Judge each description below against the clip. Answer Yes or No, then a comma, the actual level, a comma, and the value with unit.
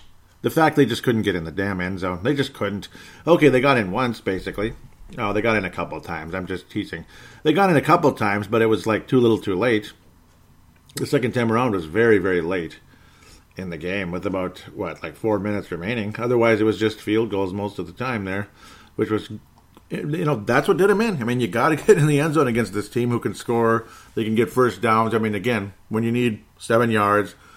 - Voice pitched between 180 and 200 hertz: No, low, 110 Hz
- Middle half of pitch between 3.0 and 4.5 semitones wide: Yes, average, 3.9 semitones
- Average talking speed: No, fast, 240 wpm